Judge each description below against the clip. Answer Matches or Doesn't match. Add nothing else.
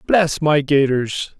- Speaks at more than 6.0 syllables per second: Doesn't match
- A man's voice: Matches